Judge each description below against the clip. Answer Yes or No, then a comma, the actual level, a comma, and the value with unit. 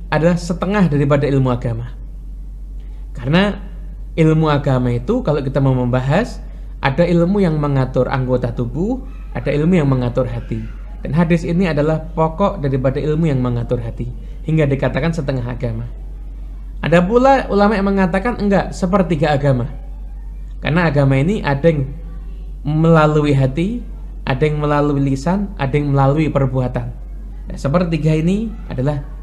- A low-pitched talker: No, medium, 150 Hz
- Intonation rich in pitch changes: No, average, 4.3 semitones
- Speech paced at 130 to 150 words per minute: Yes, average, 135 wpm